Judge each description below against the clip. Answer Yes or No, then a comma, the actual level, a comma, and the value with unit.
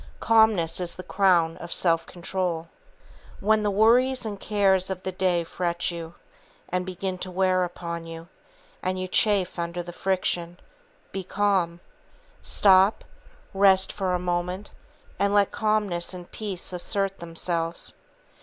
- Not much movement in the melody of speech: Yes, narrow, 2.3 semitones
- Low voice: No, medium, 185 Hz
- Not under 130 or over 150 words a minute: Yes, average, 140 wpm